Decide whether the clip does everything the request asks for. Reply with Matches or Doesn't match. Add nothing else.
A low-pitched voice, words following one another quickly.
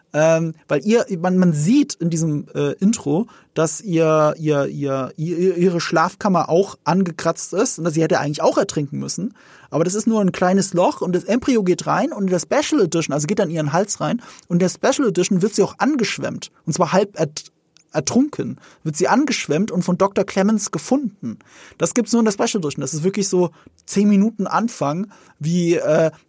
Doesn't match